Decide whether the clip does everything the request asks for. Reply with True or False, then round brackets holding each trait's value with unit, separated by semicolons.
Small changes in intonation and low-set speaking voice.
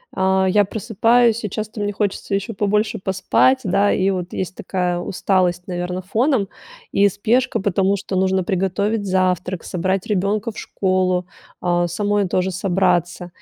False (2.2 semitones; 190 Hz)